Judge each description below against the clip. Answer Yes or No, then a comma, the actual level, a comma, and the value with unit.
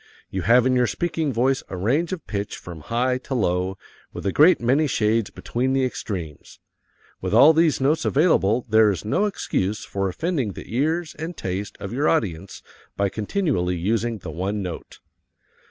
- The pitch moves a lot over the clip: Yes, wide, 6.6 semitones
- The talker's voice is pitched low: Yes, low, 115 Hz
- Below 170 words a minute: No, average, 175 wpm